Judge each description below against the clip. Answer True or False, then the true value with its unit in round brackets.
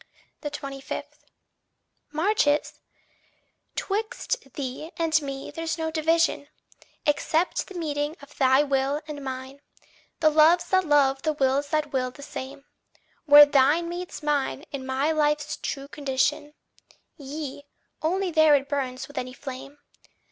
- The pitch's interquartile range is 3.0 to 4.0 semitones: False (2.5 semitones)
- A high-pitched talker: True (290 Hz)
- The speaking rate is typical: False (130 wpm)